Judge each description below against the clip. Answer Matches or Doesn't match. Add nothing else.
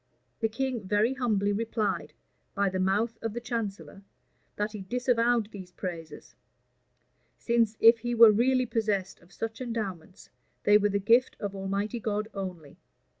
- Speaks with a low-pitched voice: Doesn't match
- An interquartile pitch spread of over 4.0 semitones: Doesn't match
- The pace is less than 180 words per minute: Matches